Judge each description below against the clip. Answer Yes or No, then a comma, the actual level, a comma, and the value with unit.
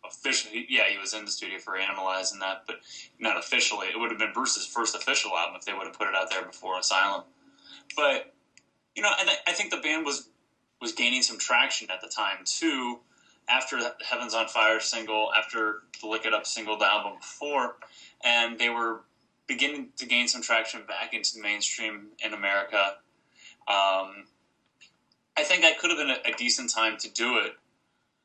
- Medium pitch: No, low, 115 Hz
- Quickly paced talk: No, average, 195 wpm